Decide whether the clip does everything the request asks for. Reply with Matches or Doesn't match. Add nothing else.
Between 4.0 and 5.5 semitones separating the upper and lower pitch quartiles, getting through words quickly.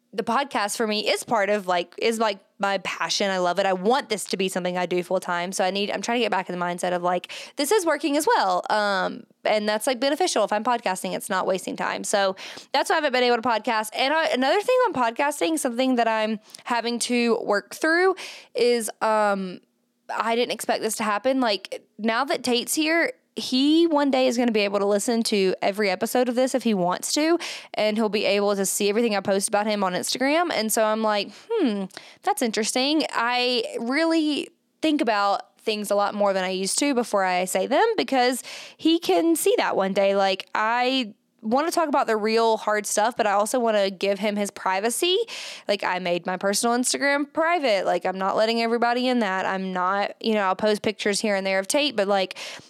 Matches